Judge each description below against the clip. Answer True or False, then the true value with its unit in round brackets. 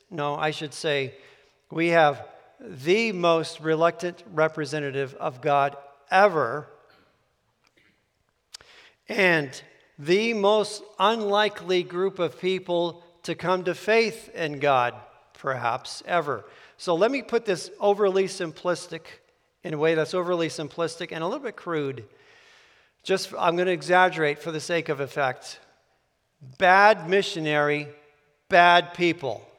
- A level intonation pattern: False (3.8 semitones)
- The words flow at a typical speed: False (120 wpm)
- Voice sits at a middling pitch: True (170 Hz)